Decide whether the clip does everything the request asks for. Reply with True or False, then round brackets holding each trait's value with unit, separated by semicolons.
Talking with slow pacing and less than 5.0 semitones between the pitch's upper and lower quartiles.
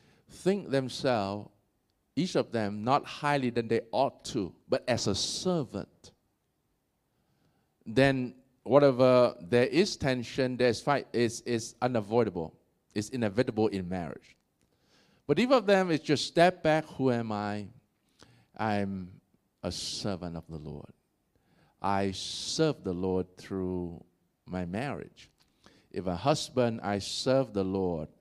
False (125 wpm; 5.6 semitones)